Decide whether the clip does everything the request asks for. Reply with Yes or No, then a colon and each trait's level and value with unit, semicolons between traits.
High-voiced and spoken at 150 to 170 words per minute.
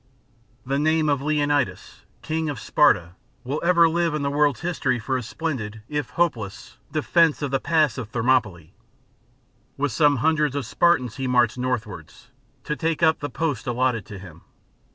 No: medium, 140 Hz; average, 165 wpm